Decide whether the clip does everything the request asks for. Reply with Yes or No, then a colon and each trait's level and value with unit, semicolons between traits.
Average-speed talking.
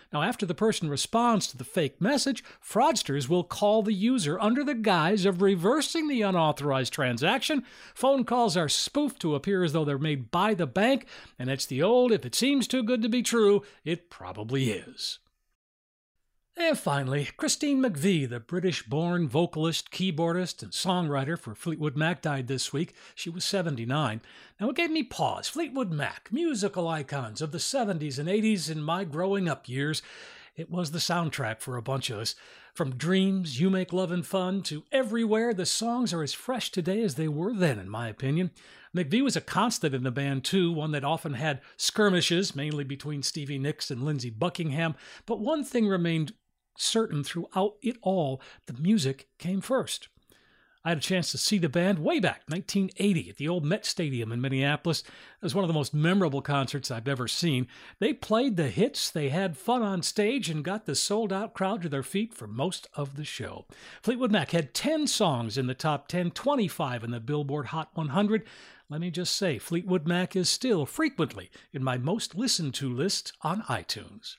Yes: average, 190 wpm